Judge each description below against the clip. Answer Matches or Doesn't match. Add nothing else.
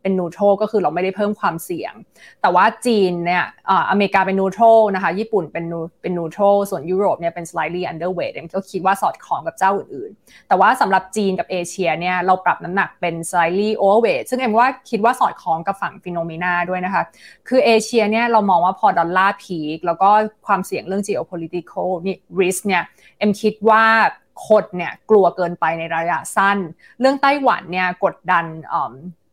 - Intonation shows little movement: Doesn't match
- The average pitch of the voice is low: Doesn't match